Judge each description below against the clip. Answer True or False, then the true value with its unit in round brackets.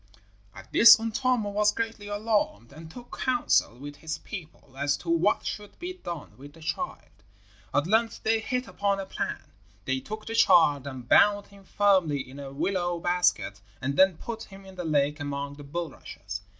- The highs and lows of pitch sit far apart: True (6.5 semitones)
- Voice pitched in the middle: True (175 Hz)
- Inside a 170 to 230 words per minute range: True (180 wpm)